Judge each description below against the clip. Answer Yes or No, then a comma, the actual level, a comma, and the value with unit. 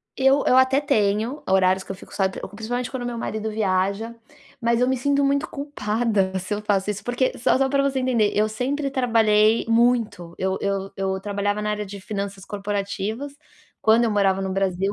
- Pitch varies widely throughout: No, average, 3.9 semitones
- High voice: Yes, high, 215 Hz